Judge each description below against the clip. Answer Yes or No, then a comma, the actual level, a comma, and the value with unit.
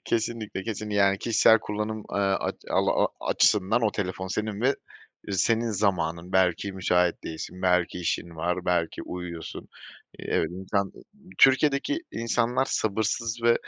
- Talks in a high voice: No, low, 100 Hz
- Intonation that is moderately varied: Yes, average, 4.0 semitones